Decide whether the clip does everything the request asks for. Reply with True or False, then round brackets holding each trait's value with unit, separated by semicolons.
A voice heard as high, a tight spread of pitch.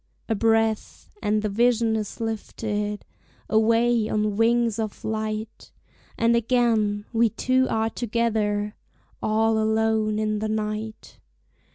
True (220 Hz; 1.2 semitones)